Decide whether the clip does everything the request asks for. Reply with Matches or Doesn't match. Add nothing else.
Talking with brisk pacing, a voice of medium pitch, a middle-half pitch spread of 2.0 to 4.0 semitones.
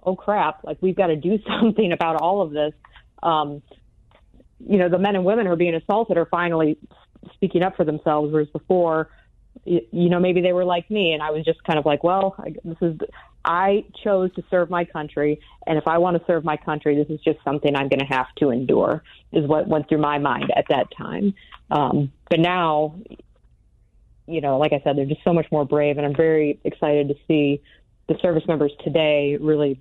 Matches